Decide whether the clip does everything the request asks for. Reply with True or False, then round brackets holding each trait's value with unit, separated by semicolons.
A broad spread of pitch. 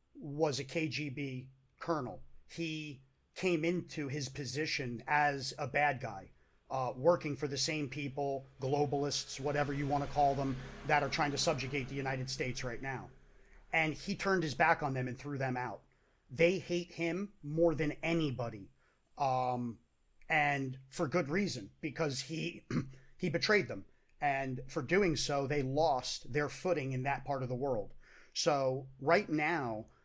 False (3.3 semitones)